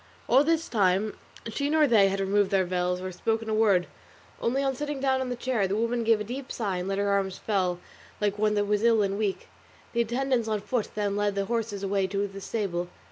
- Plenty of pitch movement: No, average, 3.2 semitones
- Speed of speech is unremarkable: No, fast, 240 wpm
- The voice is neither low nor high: No, high, 210 Hz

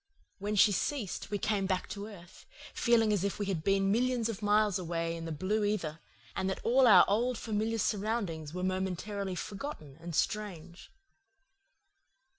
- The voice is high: Yes, high, 200 Hz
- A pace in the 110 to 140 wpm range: No, average, 165 wpm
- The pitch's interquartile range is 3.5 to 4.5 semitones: No, average, 3.1 semitones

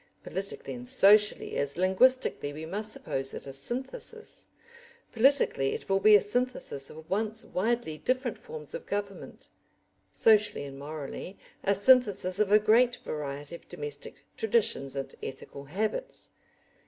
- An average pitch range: No, wide, 8.1 semitones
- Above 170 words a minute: No, average, 140 wpm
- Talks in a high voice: Yes, high, 200 Hz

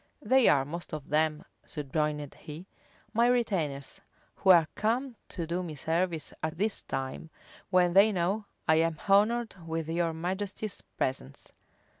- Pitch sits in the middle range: Yes, medium, 170 Hz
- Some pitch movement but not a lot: Yes, average, 4.6 semitones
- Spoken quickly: No, average, 145 wpm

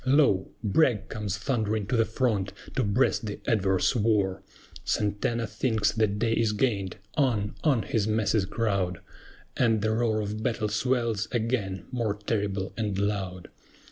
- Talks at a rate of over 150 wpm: No, average, 145 wpm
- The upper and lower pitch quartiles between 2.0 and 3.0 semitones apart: Yes, narrow, 2.5 semitones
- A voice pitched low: Yes, low, 110 Hz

